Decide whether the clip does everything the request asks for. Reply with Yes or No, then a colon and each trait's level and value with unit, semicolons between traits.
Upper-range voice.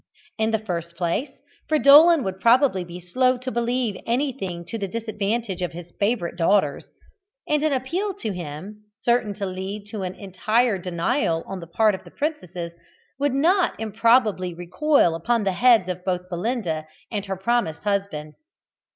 Yes: high, 205 Hz